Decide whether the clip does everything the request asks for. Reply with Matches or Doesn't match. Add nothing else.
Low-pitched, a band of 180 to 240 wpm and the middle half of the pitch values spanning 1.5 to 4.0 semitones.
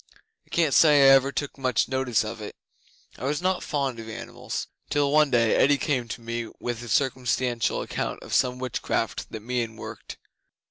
Matches